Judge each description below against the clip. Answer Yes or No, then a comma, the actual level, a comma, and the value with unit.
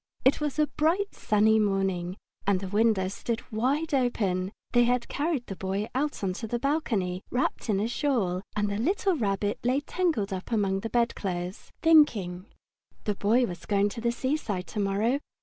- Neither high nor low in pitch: No, high, 220 Hz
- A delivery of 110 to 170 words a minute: No, average, 180 wpm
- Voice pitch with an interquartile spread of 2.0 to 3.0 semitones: No, average, 5.1 semitones